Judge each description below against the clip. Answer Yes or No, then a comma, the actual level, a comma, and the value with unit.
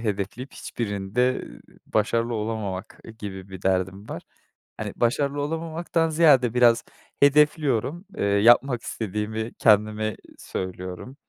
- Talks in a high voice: No, low, 115 Hz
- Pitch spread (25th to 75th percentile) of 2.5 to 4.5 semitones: No, average, 5.2 semitones